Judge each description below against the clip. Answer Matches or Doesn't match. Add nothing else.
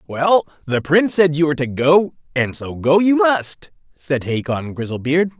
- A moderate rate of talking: Matches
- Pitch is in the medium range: Matches